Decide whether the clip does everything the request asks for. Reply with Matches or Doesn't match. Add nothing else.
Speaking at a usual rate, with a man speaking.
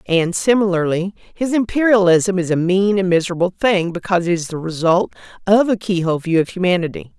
Doesn't match